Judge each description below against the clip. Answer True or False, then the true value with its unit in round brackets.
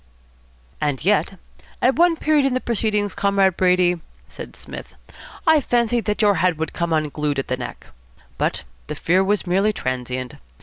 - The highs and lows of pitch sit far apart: True (5.7 semitones)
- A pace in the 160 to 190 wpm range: True (165 wpm)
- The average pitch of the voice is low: False (190 Hz)